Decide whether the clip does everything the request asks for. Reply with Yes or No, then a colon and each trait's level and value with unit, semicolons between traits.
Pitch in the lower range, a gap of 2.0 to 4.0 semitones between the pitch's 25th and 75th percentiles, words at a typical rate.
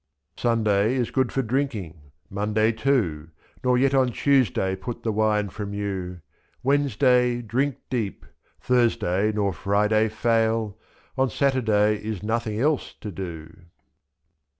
No: low, 110 Hz; average, 3.6 semitones; slow, 125 wpm